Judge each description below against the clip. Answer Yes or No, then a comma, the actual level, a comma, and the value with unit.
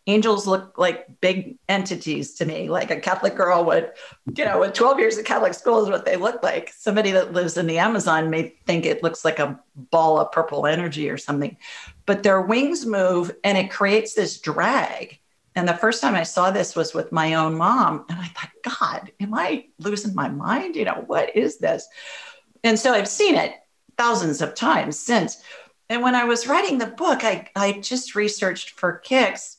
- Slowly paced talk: No, fast, 205 wpm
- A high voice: Yes, high, 200 Hz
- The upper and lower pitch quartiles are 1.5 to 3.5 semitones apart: No, wide, 5.6 semitones